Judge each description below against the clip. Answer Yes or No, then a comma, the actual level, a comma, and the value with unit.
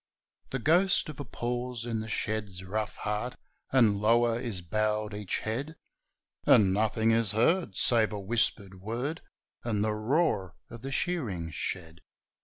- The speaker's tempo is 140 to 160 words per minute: Yes, average, 150 wpm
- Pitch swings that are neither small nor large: Yes, average, 3.0 semitones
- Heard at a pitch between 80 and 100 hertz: No, low, 110 Hz